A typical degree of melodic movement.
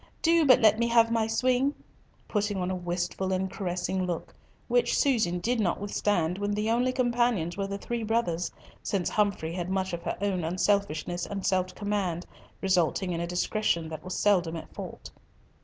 Yes: average, 4.0 semitones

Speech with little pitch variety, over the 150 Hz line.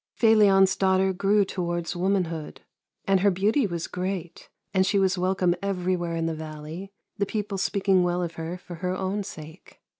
Yes: narrow, 2.2 semitones; medium, 185 Hz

